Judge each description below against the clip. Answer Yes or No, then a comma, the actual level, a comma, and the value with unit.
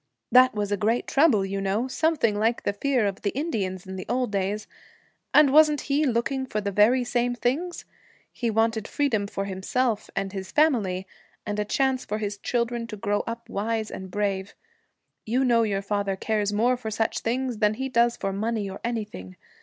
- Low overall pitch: No, high, 220 Hz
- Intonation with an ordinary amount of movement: Yes, average, 3.7 semitones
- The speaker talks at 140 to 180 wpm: No, average, 195 wpm